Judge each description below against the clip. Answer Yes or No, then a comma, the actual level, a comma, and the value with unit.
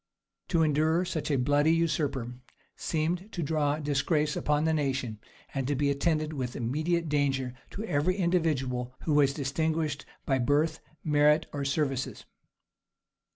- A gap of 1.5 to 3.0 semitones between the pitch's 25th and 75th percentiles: Yes, narrow, 2.6 semitones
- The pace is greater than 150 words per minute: No, average, 140 wpm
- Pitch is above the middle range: No, medium, 150 Hz